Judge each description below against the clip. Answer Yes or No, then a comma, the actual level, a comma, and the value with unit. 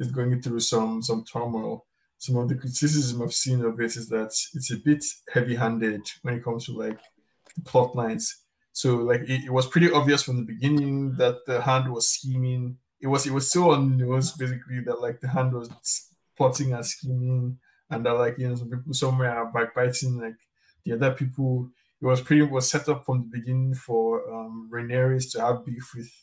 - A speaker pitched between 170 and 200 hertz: No, low, 125 Hz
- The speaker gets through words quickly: Yes, fast, 210 wpm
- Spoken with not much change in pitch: Yes, narrow, 2.1 semitones